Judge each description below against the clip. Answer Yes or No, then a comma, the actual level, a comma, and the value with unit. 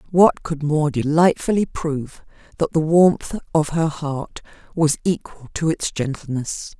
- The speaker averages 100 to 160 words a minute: Yes, average, 140 wpm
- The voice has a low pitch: No, medium, 155 Hz